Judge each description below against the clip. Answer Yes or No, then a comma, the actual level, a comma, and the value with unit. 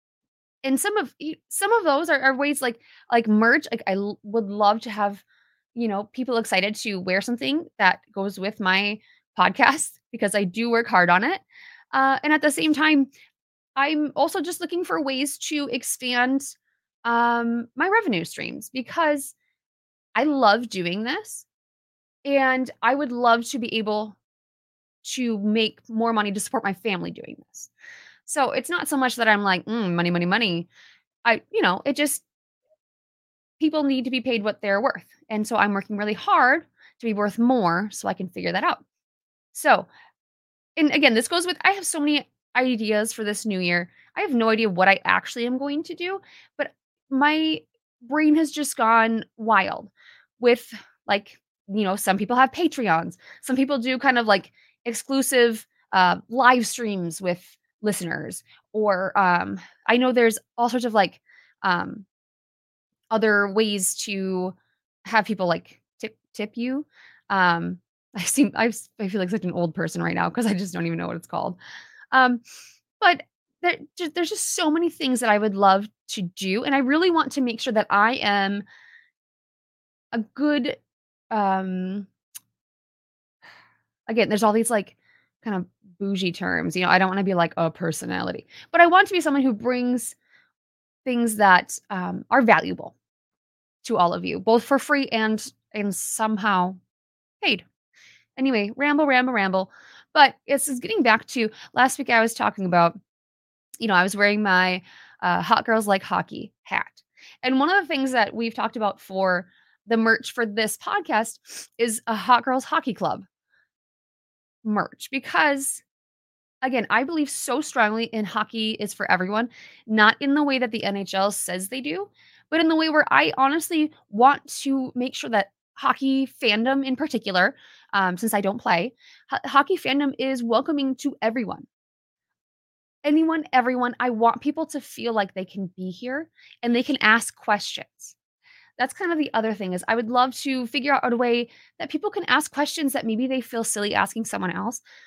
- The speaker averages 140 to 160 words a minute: No, average, 175 wpm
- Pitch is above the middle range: Yes, high, 235 Hz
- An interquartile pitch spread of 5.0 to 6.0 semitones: Yes, average, 5.3 semitones